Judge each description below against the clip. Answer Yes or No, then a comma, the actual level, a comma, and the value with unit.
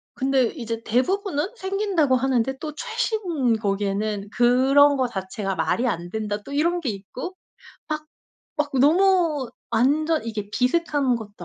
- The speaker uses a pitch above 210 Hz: Yes, very high, 260 Hz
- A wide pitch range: Yes, wide, 6.0 semitones